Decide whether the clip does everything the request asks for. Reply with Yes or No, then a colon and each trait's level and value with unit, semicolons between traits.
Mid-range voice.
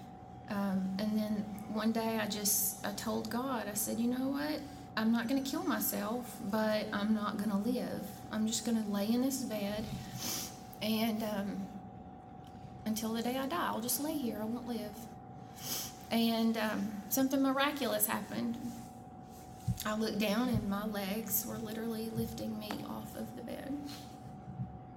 No: high, 220 Hz